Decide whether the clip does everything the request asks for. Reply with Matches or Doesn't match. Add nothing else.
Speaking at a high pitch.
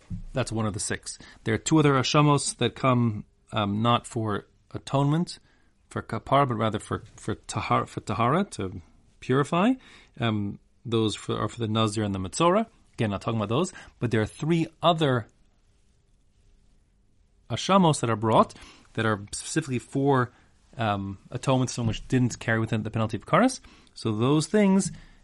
Doesn't match